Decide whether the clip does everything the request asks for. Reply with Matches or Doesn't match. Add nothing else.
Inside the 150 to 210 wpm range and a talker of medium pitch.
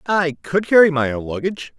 Matches